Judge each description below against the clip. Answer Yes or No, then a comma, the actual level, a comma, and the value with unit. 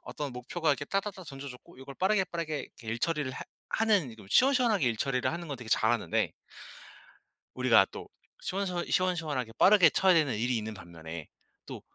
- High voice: No, medium, 145 Hz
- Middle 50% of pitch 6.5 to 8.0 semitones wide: Yes, wide, 6.8 semitones